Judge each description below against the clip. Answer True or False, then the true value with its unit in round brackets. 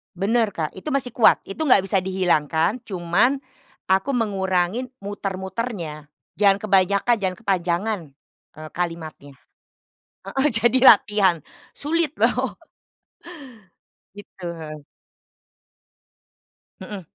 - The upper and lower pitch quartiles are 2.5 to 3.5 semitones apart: False (4.3 semitones)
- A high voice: True (195 Hz)